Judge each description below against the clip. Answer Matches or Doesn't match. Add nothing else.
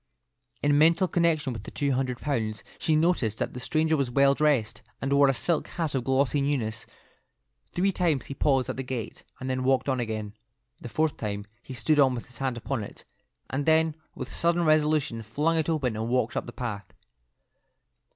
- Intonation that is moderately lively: Matches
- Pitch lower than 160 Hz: Matches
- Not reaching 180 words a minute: Doesn't match